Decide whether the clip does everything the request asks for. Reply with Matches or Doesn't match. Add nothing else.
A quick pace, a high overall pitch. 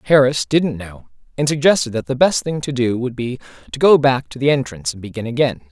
Doesn't match